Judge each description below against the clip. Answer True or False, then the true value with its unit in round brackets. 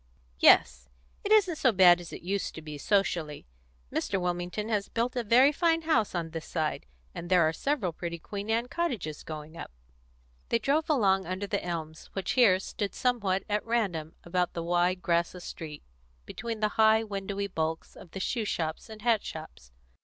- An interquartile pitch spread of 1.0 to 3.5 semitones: False (4.9 semitones)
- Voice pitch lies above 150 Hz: True (190 Hz)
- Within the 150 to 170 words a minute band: False (185 wpm)